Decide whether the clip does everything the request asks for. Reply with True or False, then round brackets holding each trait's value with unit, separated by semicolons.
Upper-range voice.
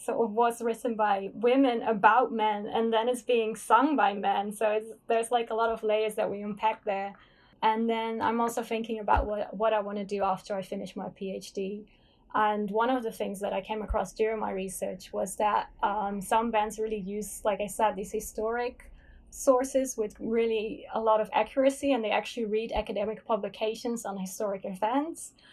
True (220 Hz)